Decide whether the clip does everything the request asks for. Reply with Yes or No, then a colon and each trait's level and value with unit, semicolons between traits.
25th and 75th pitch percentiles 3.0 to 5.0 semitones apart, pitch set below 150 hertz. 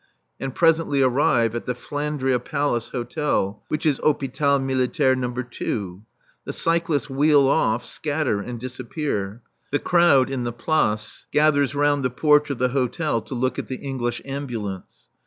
Yes: average, 3.3 semitones; low, 135 Hz